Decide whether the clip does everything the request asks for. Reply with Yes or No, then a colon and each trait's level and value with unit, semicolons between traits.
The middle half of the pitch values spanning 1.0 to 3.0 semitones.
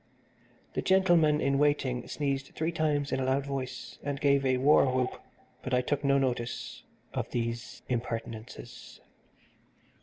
Yes: narrow, 2.4 semitones